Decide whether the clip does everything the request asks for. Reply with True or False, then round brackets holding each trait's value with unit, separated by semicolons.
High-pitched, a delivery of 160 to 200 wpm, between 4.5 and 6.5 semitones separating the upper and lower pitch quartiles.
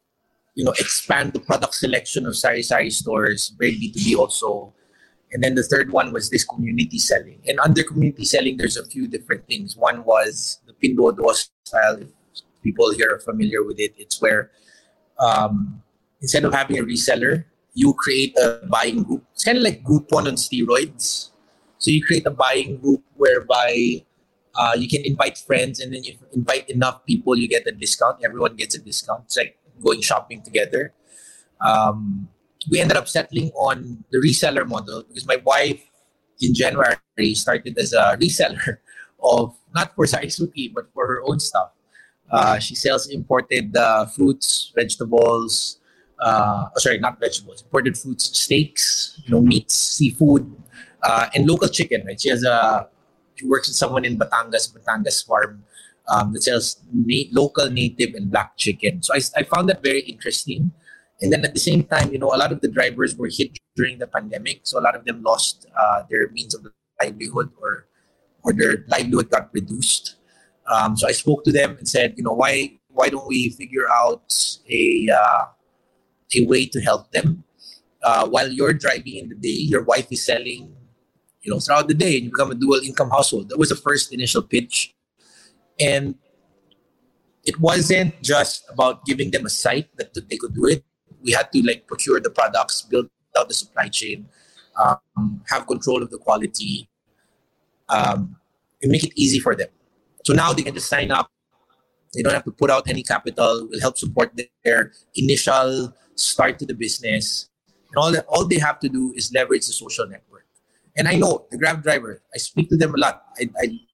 False (140 Hz; 185 wpm; 5.1 semitones)